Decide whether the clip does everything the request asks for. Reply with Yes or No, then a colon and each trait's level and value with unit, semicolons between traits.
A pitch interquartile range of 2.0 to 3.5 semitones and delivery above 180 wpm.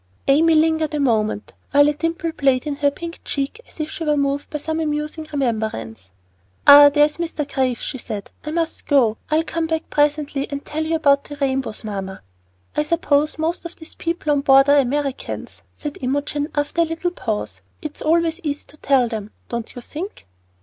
Yes: average, 2.7 semitones; average, 190 wpm